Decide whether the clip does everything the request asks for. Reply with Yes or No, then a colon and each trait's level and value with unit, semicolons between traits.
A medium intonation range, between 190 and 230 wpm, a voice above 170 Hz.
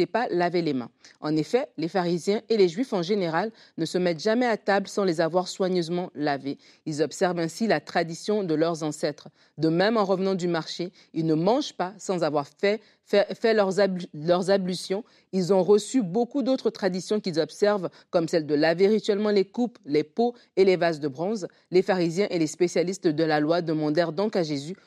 Yes: average, 3.8 semitones; average, 200 wpm; medium, 185 Hz